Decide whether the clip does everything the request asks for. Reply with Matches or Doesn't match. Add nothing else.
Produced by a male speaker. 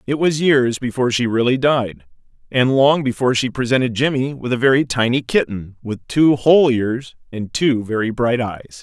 Matches